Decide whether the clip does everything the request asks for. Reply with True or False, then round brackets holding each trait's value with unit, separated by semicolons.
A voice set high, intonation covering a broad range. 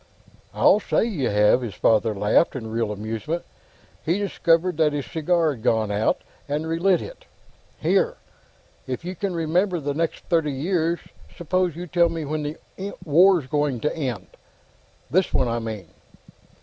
False (155 Hz; 6.5 semitones)